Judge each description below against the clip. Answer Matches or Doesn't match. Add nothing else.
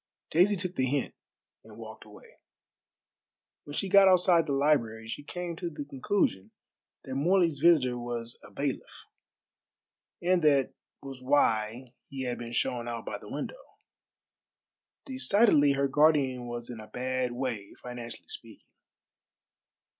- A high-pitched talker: Doesn't match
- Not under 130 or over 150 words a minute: Matches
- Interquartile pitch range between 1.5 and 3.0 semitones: Doesn't match